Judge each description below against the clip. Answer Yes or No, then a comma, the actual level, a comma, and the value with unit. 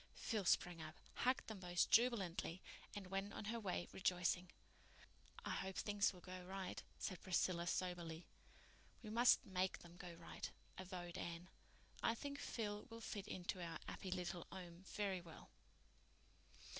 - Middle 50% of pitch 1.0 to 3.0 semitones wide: Yes, narrow, 2.6 semitones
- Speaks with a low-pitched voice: No, medium, 185 Hz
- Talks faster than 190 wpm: No, average, 150 wpm